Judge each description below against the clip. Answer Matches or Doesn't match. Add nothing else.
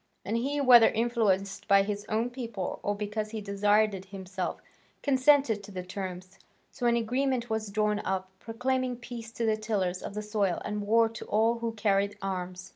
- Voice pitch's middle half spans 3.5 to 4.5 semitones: Doesn't match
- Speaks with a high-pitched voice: Matches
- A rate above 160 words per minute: Matches